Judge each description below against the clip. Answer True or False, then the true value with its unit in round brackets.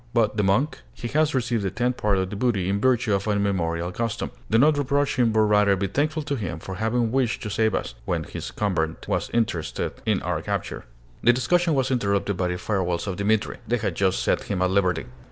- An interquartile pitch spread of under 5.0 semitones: True (4.1 semitones)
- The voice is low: True (105 Hz)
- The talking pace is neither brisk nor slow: False (225 wpm)